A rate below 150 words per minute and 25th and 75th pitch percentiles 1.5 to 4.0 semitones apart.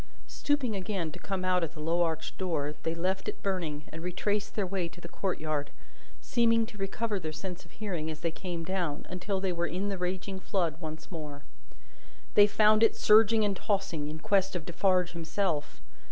No: average, 195 wpm; average, 3.5 semitones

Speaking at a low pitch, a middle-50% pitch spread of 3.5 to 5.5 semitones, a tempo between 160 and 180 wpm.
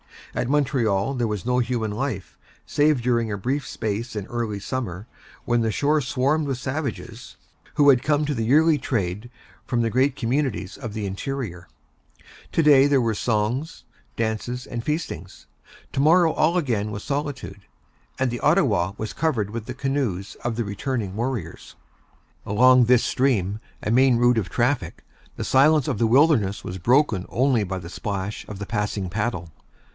Yes: low, 120 Hz; average, 4.7 semitones; average, 170 wpm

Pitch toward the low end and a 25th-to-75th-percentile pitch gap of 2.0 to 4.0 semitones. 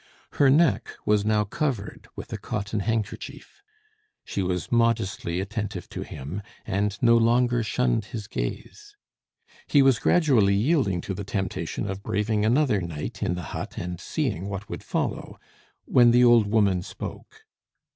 Yes: low, 105 Hz; average, 3.5 semitones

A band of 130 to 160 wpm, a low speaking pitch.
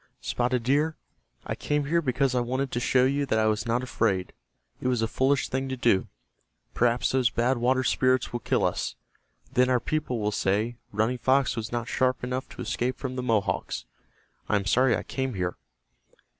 No: average, 195 wpm; low, 125 Hz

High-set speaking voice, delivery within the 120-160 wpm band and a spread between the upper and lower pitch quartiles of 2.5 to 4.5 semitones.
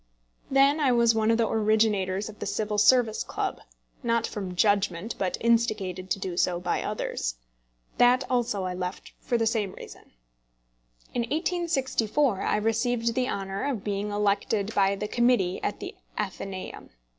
Yes: high, 215 Hz; average, 155 wpm; average, 3.4 semitones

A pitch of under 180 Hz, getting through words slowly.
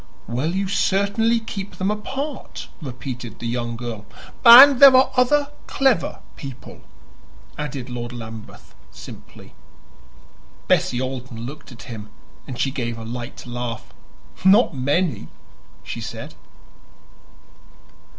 Yes: low, 135 Hz; slow, 115 wpm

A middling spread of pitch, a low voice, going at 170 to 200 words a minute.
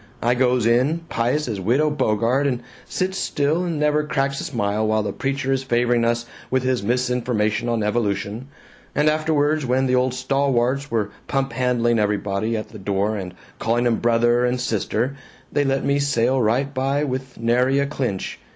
Yes: average, 3.0 semitones; low, 125 Hz; average, 175 wpm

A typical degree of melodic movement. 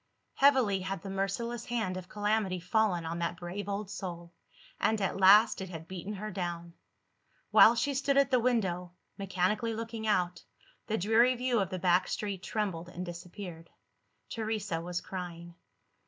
Yes: average, 3.7 semitones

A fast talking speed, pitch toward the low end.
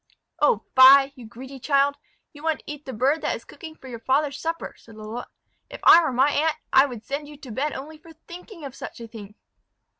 No: fast, 230 wpm; very high, 275 Hz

